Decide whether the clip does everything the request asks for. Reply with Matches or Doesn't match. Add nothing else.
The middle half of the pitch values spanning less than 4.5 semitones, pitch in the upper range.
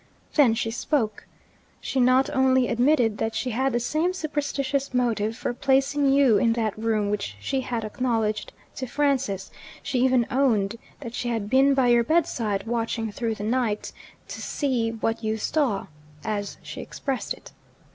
Matches